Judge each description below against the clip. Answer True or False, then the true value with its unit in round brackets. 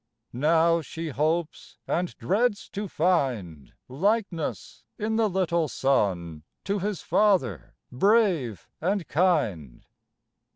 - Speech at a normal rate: False (100 wpm)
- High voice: False (165 Hz)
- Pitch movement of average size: False (7.3 semitones)